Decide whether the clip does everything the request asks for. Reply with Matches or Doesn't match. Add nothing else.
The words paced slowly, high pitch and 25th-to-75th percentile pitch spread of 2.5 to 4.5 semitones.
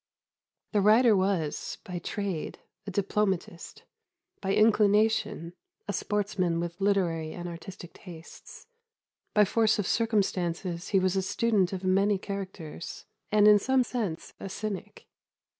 Matches